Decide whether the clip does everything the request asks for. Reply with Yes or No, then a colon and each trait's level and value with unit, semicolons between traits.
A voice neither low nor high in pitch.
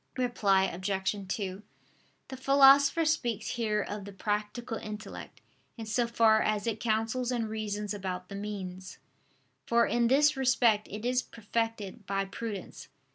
No: high, 215 Hz